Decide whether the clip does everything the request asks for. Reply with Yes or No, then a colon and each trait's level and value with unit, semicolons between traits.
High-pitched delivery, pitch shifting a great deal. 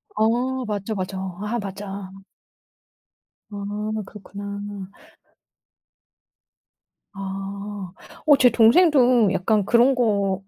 No: high, 205 Hz; average, 3.1 semitones